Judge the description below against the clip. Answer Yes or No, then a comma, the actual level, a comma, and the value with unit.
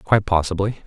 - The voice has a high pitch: No, very low, 95 Hz